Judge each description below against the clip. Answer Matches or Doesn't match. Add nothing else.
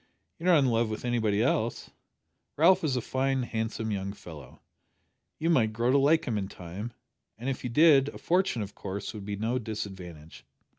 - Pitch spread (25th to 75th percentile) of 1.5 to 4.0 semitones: Doesn't match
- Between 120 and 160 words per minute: Doesn't match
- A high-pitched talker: Doesn't match